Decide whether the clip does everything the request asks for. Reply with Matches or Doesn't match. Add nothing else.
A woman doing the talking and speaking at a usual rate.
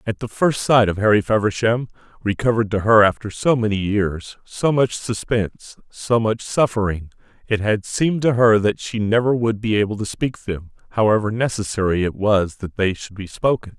Doesn't match